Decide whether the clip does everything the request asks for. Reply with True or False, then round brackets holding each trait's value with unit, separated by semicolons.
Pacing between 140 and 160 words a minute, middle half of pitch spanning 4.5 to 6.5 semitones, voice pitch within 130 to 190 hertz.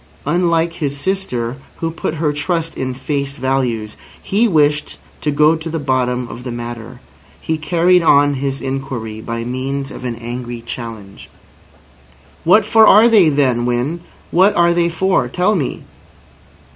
True (155 wpm; 5.3 semitones; 140 Hz)